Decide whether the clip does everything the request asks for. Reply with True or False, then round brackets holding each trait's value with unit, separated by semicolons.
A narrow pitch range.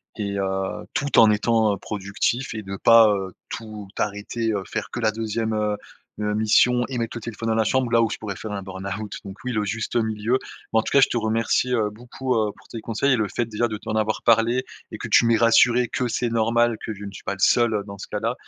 True (2.0 semitones)